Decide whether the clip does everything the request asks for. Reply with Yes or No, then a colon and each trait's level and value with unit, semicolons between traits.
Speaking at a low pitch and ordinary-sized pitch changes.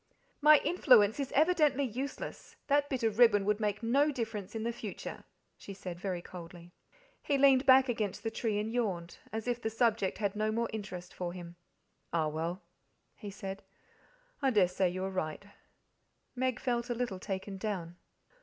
No: high, 215 Hz; average, 4.7 semitones